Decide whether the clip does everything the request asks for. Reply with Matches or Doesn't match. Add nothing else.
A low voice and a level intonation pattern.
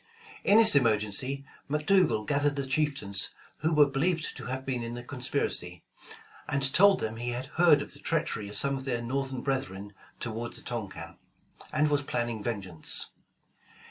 Doesn't match